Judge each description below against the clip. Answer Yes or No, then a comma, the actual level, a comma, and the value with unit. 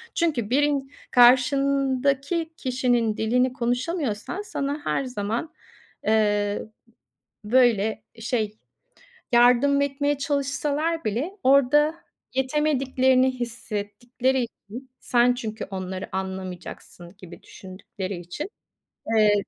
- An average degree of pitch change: Yes, average, 4.5 semitones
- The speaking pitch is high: Yes, very high, 250 Hz